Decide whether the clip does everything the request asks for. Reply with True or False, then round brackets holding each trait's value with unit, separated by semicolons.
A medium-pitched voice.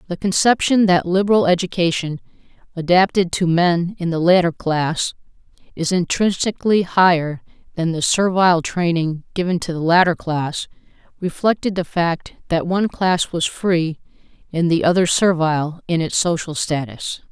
True (175 Hz)